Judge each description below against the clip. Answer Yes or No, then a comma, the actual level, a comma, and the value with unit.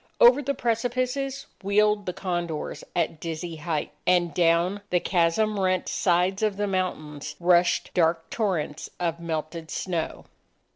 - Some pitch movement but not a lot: Yes, average, 3.7 semitones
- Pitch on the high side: No, medium, 180 Hz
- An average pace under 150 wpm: Yes, slow, 135 wpm